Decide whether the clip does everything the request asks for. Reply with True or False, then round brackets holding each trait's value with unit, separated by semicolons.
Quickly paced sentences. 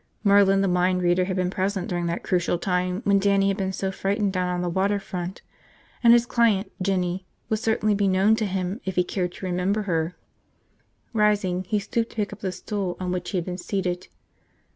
True (210 wpm)